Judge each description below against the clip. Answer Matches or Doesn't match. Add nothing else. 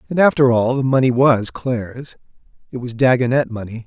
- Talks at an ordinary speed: Matches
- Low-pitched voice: Matches